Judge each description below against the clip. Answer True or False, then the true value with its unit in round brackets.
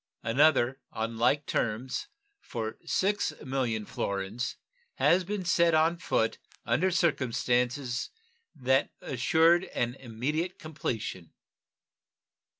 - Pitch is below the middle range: True (130 Hz)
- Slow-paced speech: True (90 wpm)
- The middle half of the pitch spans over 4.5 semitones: True (5.6 semitones)